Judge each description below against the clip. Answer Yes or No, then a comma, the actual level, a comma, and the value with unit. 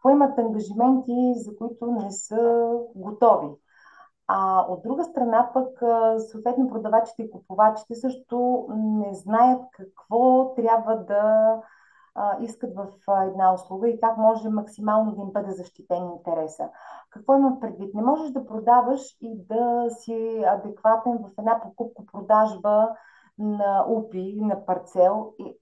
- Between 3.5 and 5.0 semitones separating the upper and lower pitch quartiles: No, average, 2.7 semitones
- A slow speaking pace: No, average, 125 wpm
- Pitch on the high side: Yes, high, 225 Hz